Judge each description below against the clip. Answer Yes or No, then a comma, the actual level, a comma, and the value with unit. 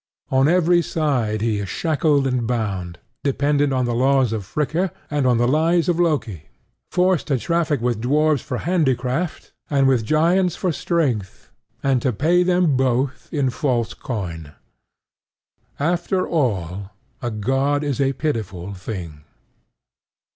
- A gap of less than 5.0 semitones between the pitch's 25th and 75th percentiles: No, wide, 5.4 semitones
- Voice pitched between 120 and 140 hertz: Yes, low, 135 Hz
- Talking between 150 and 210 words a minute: No, average, 140 wpm